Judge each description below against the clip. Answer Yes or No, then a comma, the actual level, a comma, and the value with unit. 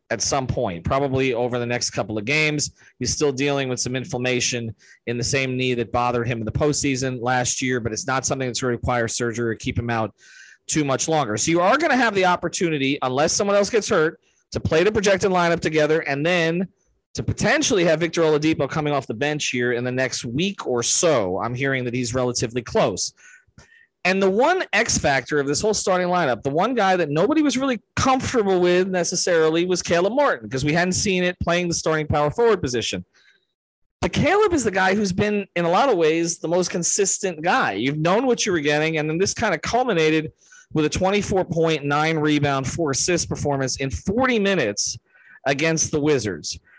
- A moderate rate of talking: No, fast, 210 wpm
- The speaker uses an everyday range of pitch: No, wide, 6.1 semitones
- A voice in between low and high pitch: Yes, medium, 150 Hz